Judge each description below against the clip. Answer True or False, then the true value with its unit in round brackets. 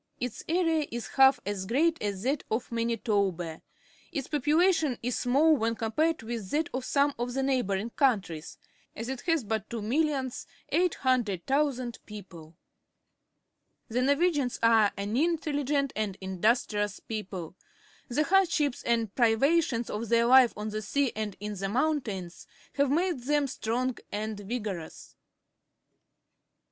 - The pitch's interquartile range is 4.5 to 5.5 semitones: True (5.2 semitones)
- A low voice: False (240 Hz)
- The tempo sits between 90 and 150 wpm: True (140 wpm)